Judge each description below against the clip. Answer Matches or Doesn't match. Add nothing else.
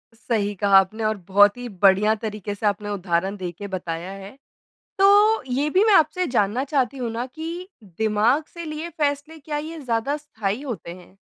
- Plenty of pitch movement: Matches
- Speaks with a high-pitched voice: Matches